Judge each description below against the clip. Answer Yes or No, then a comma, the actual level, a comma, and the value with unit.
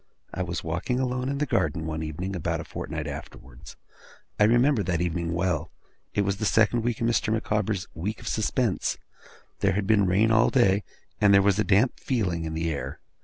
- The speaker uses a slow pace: No, average, 195 wpm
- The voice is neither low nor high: No, low, 100 Hz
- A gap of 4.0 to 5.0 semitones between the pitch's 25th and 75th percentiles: Yes, average, 4.5 semitones